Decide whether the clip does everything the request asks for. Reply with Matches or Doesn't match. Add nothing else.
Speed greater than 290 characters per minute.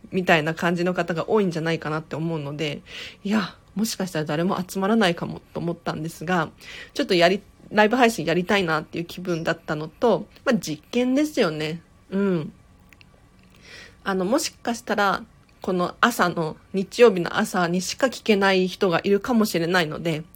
Matches